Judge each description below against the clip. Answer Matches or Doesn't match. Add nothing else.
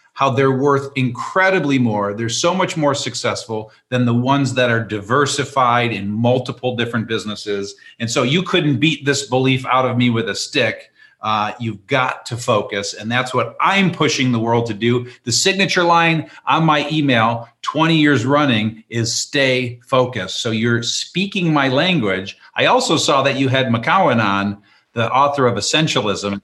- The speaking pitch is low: Matches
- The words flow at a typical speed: Matches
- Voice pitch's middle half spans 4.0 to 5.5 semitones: Doesn't match